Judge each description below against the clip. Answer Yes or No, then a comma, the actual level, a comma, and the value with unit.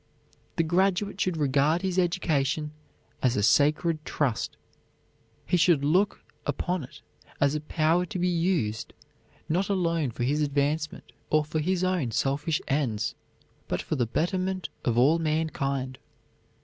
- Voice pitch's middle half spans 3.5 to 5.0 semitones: Yes, average, 4.2 semitones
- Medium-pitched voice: Yes, medium, 155 Hz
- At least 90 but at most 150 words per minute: Yes, average, 140 wpm